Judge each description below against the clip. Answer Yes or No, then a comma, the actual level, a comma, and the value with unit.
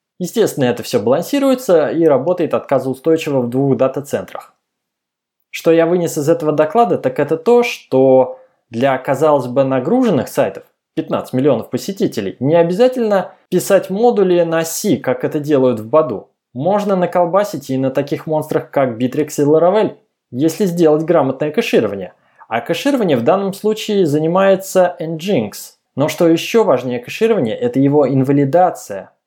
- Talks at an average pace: Yes, average, 140 wpm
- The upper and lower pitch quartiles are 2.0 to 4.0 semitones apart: No, average, 5.3 semitones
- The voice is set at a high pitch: No, medium, 165 Hz